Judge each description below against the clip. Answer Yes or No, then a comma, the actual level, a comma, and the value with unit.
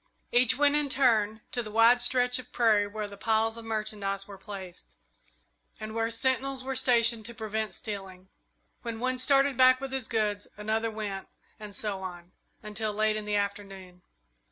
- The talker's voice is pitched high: Yes, high, 220 Hz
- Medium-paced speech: Yes, average, 175 wpm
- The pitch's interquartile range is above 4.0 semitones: No, average, 3.1 semitones